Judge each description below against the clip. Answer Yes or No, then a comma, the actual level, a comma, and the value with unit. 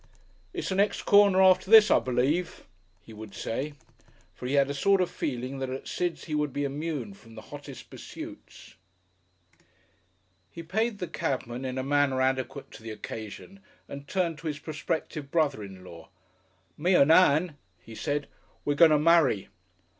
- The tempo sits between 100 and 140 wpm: No, average, 170 wpm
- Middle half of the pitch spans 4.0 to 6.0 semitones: Yes, average, 4.6 semitones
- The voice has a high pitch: No, medium, 145 Hz